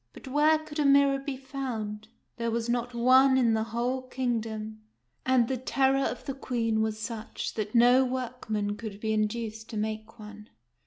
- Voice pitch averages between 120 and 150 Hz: No, high, 235 Hz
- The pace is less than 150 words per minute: No, average, 180 wpm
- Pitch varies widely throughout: No, average, 3.2 semitones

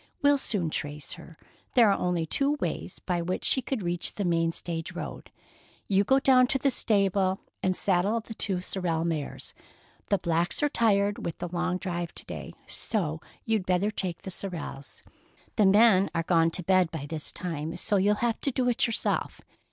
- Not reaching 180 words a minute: No, average, 190 wpm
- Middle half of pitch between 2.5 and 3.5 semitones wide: No, average, 4.0 semitones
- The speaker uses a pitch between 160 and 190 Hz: Yes, medium, 185 Hz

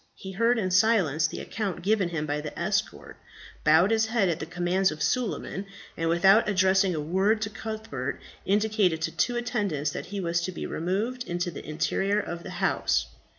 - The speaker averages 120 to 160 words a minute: No, average, 190 wpm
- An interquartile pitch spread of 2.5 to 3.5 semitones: No, average, 4.3 semitones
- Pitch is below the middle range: No, high, 190 Hz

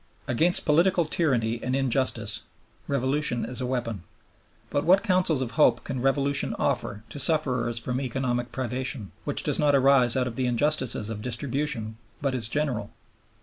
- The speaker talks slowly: No, average, 155 wpm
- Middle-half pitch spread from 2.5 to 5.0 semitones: Yes, average, 3.4 semitones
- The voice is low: Yes, low, 130 Hz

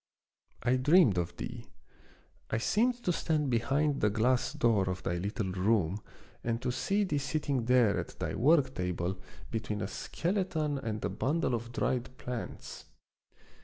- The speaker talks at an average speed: Yes, average, 155 wpm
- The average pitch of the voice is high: No, low, 120 Hz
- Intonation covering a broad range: Yes, wide, 5.9 semitones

